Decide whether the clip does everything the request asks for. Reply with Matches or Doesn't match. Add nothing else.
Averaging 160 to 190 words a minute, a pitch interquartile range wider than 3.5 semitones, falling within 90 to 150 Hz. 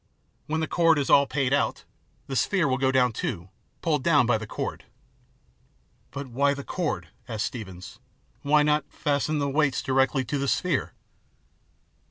Doesn't match